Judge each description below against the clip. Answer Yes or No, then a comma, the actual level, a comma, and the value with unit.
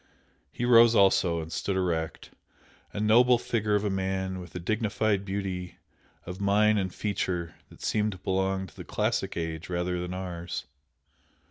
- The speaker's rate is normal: Yes, average, 160 wpm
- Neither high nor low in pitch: No, very low, 95 Hz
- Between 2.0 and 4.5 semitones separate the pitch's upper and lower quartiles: Yes, average, 2.8 semitones